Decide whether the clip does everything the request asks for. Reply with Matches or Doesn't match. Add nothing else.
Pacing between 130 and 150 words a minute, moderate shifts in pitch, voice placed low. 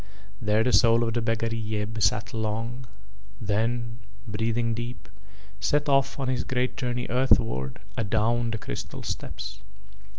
Doesn't match